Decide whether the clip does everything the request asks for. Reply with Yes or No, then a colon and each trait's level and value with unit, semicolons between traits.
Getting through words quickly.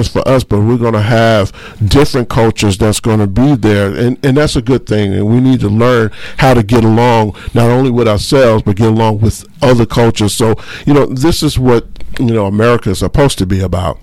Yes: fast, 225 wpm